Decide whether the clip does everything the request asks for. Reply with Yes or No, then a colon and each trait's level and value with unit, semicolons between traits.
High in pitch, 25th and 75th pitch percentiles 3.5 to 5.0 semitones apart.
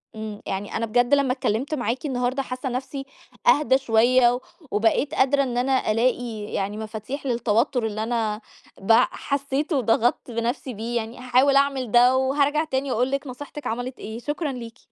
No: very high, 250 Hz; average, 3.1 semitones